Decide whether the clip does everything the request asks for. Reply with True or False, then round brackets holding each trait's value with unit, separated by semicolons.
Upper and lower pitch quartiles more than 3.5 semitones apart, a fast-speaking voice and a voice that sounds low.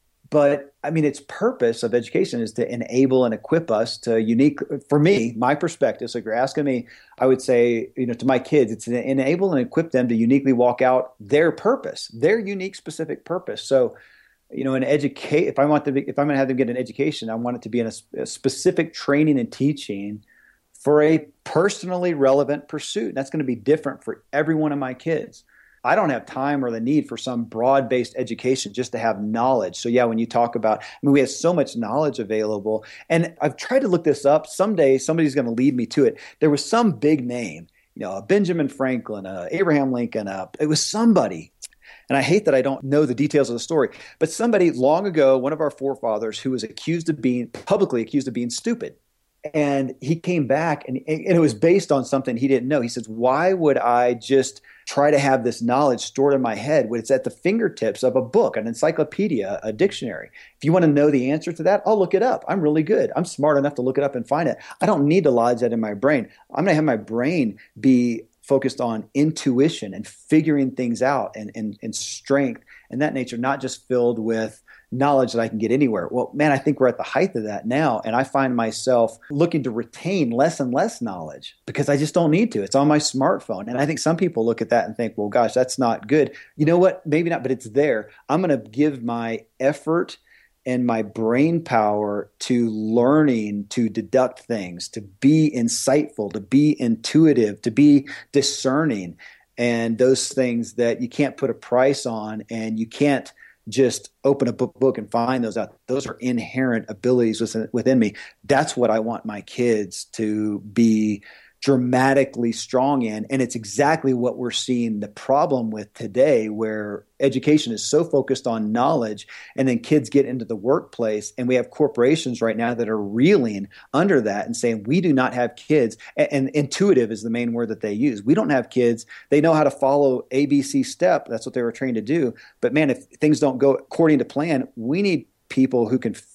True (4.1 semitones; 220 wpm; 130 Hz)